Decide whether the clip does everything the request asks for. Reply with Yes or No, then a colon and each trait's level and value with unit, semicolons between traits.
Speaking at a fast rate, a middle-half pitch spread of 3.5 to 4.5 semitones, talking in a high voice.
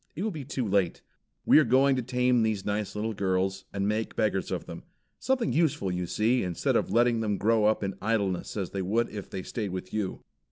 No: fast, 225 wpm; average, 4.0 semitones; low, 110 Hz